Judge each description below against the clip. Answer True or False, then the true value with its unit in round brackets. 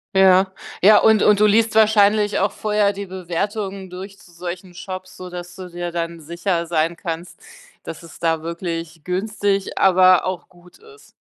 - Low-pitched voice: False (185 Hz)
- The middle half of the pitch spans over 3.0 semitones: False (2.7 semitones)